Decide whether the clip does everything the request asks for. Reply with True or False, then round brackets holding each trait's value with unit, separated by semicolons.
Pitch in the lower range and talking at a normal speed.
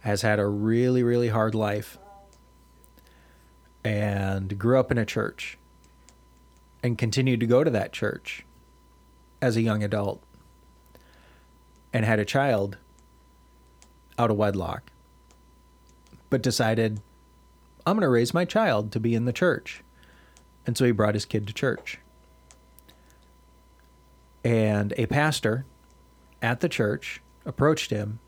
False (90 Hz; 125 wpm)